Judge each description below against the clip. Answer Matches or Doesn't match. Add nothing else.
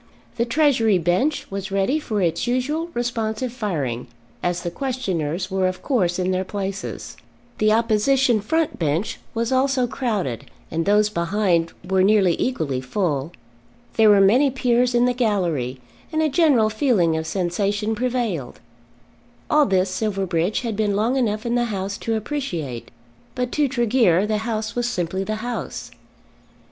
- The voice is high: Matches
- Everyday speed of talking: Matches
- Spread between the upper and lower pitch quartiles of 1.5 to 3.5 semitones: Doesn't match